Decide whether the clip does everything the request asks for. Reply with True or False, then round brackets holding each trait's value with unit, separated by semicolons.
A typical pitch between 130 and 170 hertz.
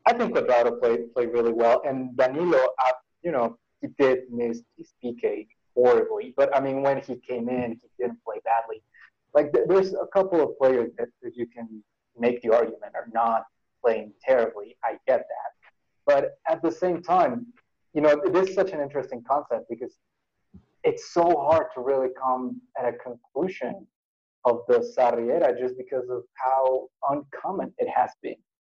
True (135 Hz)